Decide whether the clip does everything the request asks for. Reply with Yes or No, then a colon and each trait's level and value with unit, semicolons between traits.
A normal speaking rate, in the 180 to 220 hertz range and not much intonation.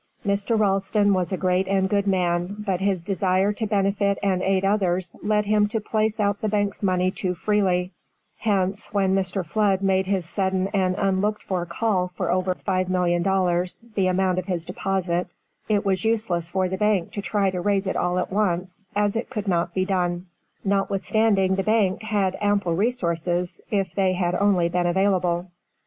Yes: average, 175 wpm; high, 190 Hz; narrow, 1.9 semitones